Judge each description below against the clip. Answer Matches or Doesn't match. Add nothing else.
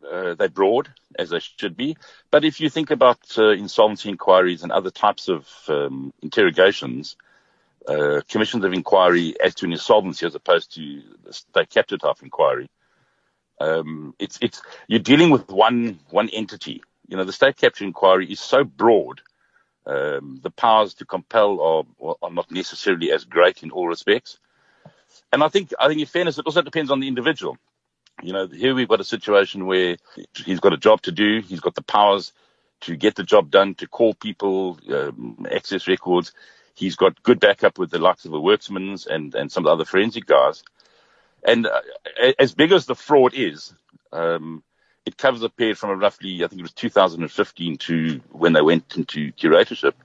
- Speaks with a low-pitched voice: Matches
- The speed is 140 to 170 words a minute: Doesn't match